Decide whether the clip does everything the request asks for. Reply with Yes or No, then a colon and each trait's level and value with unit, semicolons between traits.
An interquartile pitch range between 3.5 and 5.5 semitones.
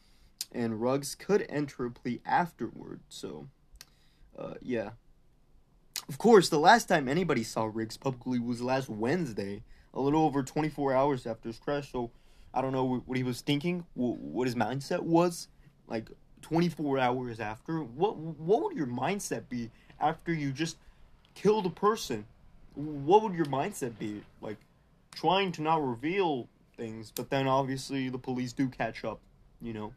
Yes: average, 4.5 semitones